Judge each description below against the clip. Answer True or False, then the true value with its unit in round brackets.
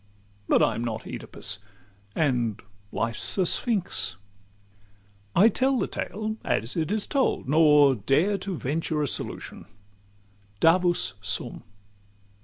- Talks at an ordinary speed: False (120 wpm)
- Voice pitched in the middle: True (150 Hz)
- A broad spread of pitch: True (8.7 semitones)